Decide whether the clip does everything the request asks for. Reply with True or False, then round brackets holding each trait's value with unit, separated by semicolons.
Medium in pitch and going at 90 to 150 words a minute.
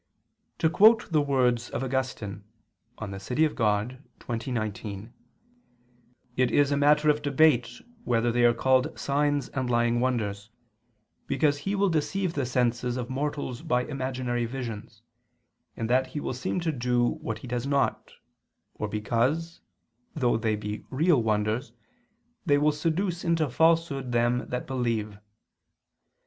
False (125 Hz; 140 wpm)